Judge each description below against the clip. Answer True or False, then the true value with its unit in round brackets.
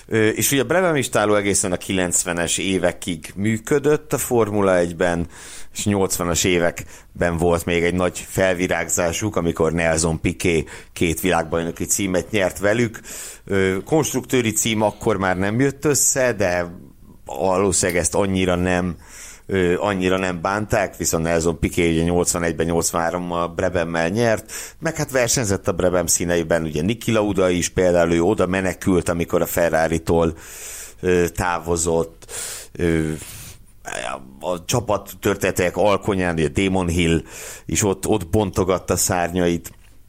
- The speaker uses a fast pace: False (120 wpm)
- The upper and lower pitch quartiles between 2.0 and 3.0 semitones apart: False (3.5 semitones)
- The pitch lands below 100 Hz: True (90 Hz)